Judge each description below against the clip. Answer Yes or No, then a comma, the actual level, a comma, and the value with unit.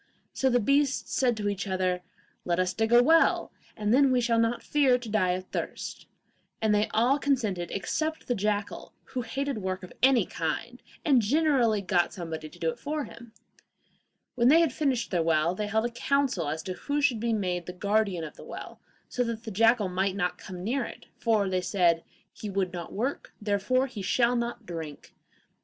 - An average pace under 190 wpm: No, average, 200 wpm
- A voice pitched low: No, high, 220 Hz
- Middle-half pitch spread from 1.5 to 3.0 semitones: No, average, 5.2 semitones